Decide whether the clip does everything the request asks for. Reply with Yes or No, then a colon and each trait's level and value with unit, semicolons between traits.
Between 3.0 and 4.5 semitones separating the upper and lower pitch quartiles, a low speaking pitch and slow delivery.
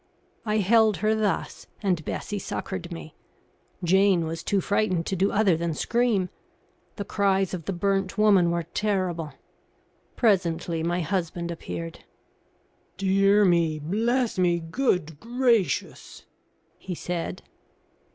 No: average, 3.3 semitones; medium, 185 Hz; slow, 120 wpm